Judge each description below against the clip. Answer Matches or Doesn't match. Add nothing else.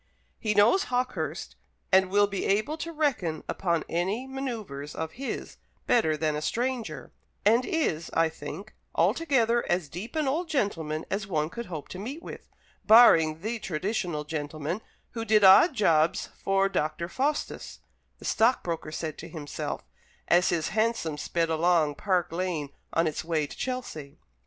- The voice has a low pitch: Doesn't match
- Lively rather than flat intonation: Matches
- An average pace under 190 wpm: Matches